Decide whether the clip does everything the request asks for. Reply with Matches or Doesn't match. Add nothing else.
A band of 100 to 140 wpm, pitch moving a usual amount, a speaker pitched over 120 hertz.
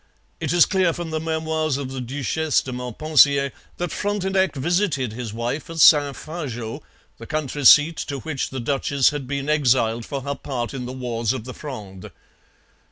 Doesn't match